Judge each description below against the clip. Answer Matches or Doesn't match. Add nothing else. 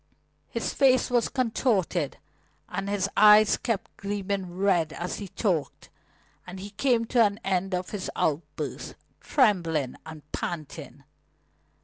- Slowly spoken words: Matches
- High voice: Matches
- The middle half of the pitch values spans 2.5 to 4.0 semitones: Matches